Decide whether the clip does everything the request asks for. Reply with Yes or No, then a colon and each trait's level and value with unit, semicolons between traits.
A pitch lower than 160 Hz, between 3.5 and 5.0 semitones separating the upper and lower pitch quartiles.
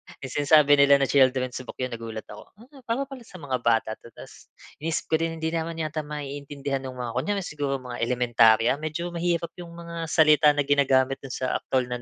Yes: medium, 140 Hz; average, 3.9 semitones